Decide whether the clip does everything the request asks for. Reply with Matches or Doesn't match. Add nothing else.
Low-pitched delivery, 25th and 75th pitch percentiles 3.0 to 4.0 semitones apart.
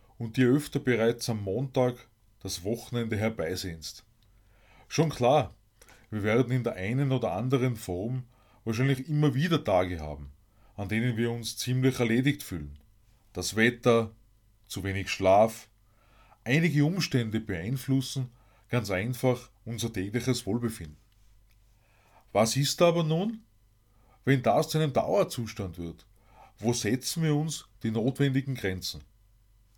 Matches